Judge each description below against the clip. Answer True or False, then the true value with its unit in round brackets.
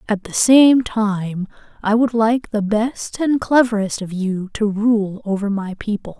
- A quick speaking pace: False (175 wpm)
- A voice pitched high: True (215 Hz)